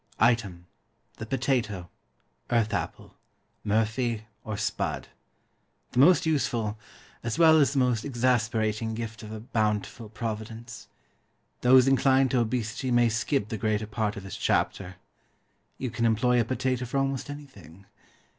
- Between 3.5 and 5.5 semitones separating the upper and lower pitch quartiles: No, average, 2.9 semitones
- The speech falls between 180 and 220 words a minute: No, slow, 135 wpm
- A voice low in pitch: Yes, low, 115 Hz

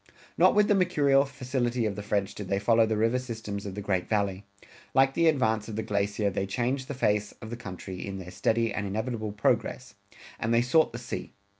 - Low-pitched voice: Yes, low, 110 Hz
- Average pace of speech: No, fast, 215 wpm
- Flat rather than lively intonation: No, average, 3.9 semitones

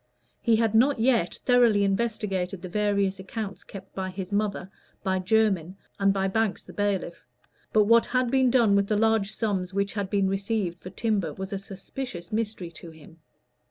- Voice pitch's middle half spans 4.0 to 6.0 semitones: No, average, 2.7 semitones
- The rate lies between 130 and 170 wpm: No, average, 180 wpm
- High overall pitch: Yes, high, 200 Hz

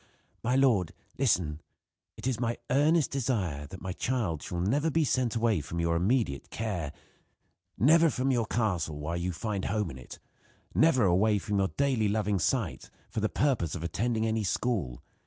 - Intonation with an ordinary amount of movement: No, wide, 6.5 semitones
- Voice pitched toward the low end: Yes, low, 110 Hz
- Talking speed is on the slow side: No, average, 175 wpm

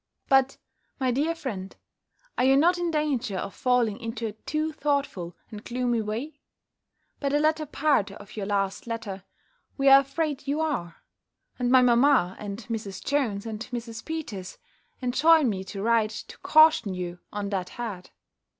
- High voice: Yes, high, 240 Hz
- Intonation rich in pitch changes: Yes, wide, 5.8 semitones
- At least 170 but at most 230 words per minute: No, average, 160 wpm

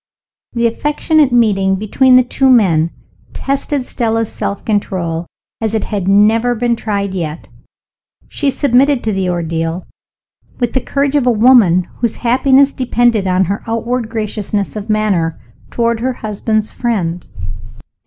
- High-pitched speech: Yes, high, 225 Hz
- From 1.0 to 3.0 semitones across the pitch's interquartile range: No, average, 4.1 semitones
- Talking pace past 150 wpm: No, average, 140 wpm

